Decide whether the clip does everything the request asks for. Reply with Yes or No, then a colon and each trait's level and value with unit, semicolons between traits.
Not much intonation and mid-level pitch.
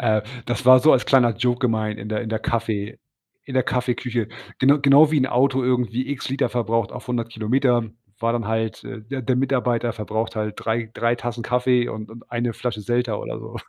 No: narrow, 2.3 semitones; low, 120 Hz